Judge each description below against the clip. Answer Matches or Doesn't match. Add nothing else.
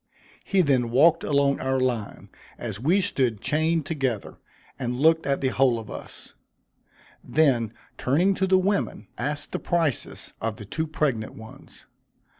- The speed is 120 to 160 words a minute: Matches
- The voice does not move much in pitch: Doesn't match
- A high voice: Doesn't match